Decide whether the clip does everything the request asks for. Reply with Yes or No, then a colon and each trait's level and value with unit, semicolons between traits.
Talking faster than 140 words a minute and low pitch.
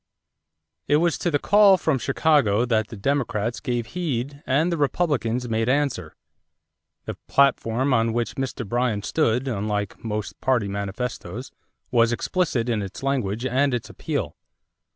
Yes: average, 150 wpm; low, 125 Hz